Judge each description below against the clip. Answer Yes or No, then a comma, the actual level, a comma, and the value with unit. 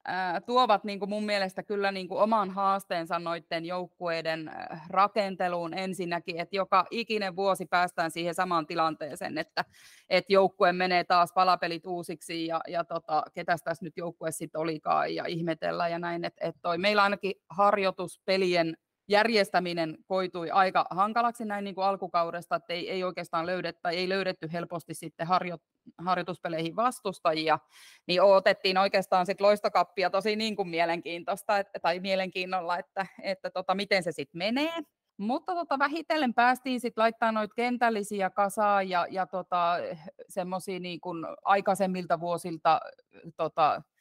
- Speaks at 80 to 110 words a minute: No, average, 140 wpm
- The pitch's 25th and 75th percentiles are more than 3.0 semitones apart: No, narrow, 2.6 semitones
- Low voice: No, medium, 185 Hz